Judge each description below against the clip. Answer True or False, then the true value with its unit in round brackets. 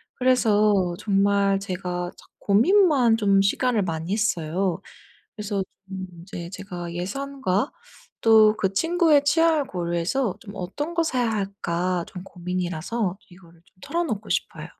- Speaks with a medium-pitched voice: False (200 Hz)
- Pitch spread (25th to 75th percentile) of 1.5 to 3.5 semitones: False (5.2 semitones)